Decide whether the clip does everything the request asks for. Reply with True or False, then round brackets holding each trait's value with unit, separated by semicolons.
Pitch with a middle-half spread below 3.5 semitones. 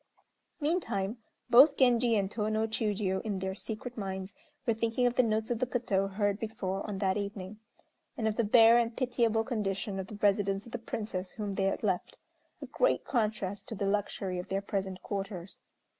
True (3.0 semitones)